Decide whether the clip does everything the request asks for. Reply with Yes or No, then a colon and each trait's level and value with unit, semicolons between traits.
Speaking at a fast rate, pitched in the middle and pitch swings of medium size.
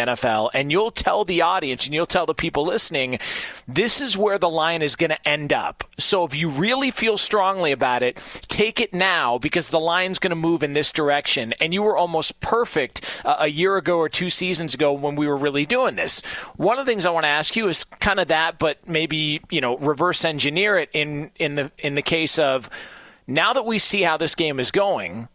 Yes: fast, 230 wpm; medium, 165 Hz; average, 4.2 semitones